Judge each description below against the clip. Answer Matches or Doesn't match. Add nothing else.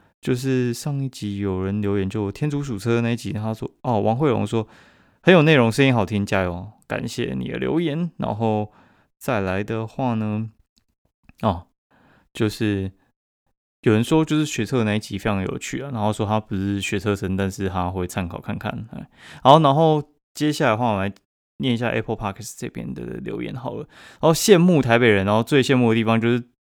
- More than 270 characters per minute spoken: Matches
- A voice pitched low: Matches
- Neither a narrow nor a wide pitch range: Matches